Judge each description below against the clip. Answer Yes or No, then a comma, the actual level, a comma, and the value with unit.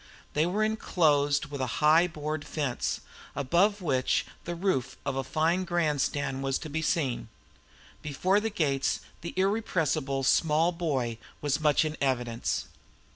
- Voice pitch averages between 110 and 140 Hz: No, medium, 150 Hz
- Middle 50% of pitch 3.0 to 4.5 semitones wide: Yes, average, 4.1 semitones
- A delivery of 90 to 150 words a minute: Yes, average, 140 wpm